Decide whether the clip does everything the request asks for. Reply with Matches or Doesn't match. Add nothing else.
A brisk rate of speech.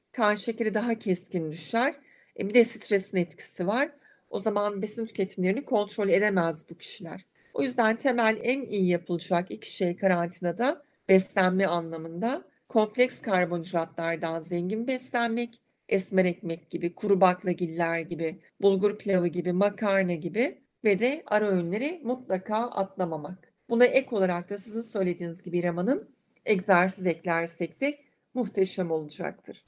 Doesn't match